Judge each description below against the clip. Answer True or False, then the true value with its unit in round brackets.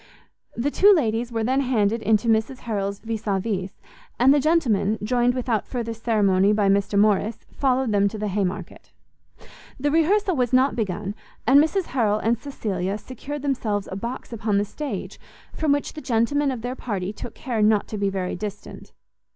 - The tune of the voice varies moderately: True (4.2 semitones)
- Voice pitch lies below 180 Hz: False (225 Hz)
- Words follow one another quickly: False (180 wpm)